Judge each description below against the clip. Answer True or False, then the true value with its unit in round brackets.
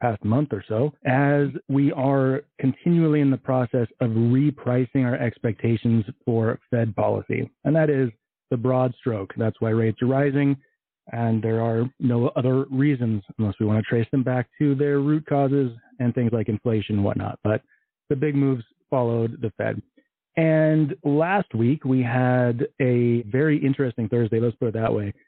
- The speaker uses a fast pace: False (175 wpm)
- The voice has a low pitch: True (125 Hz)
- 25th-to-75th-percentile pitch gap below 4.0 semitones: True (3.4 semitones)